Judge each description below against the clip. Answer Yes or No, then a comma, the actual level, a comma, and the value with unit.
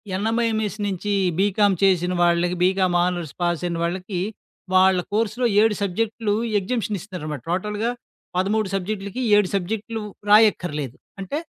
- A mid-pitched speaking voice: No, high, 195 Hz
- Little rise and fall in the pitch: No, average, 3.2 semitones